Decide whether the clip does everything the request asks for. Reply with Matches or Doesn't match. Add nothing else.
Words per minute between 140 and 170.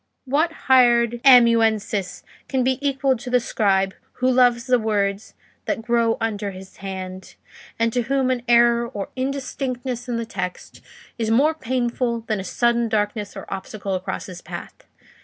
Matches